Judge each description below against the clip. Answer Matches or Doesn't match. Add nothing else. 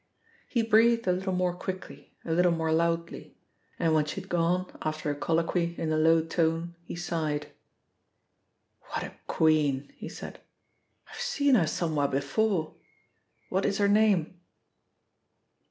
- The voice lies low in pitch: Doesn't match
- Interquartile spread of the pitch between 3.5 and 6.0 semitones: Doesn't match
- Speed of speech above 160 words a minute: Doesn't match